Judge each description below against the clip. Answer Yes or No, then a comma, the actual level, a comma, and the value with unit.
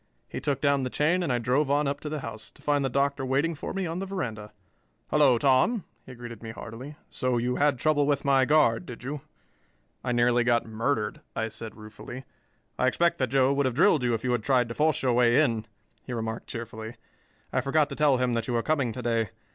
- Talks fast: Yes, fast, 235 wpm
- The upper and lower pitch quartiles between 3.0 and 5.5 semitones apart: Yes, average, 3.6 semitones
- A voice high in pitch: No, low, 130 Hz